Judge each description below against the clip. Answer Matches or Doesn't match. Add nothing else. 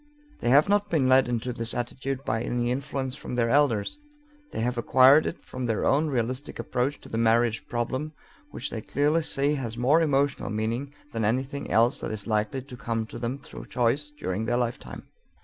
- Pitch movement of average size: Matches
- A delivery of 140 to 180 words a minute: Doesn't match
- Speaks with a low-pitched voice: Matches